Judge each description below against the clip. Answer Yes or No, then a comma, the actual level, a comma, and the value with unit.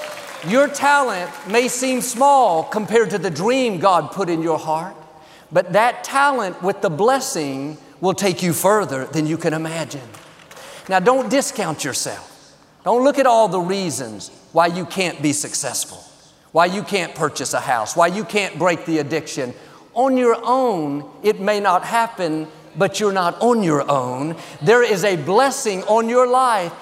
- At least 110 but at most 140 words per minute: No, average, 170 wpm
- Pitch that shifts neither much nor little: No, wide, 6.5 semitones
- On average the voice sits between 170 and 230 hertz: Yes, medium, 185 Hz